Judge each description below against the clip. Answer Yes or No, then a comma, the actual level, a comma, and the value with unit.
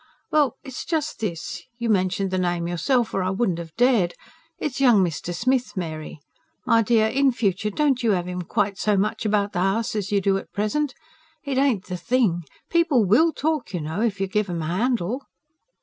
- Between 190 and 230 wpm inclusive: Yes, average, 200 wpm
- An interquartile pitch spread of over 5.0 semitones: Yes, wide, 5.5 semitones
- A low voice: No, high, 210 Hz